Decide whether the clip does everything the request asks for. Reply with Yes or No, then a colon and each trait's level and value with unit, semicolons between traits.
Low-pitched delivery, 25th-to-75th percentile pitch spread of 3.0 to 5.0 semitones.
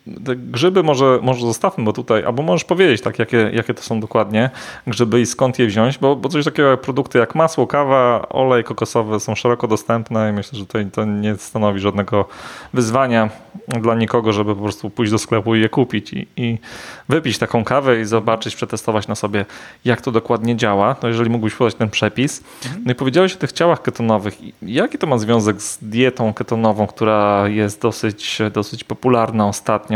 No: low, 115 Hz; narrow, 2.6 semitones